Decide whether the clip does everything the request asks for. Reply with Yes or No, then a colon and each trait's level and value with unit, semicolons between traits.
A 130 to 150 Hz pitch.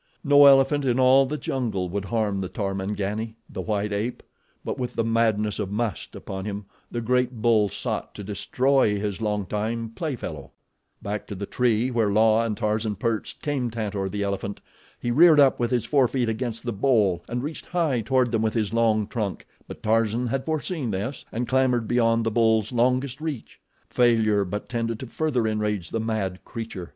No: low, 115 Hz